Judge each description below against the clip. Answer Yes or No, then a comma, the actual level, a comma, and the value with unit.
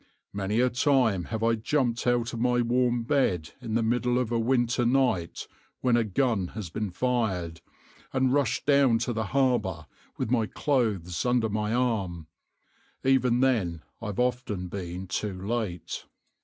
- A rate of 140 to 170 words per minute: Yes, average, 155 wpm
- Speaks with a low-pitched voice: Yes, low, 115 Hz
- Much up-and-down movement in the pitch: No, average, 4.1 semitones